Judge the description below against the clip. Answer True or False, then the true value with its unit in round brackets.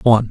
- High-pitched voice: False (115 Hz)